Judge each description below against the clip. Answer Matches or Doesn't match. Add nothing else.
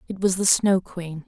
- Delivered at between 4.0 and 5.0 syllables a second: Matches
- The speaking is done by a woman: Matches